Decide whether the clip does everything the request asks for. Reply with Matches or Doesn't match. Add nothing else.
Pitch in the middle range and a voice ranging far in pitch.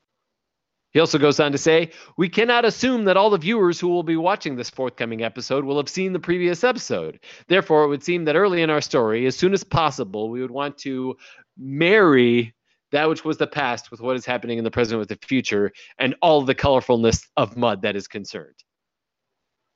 Matches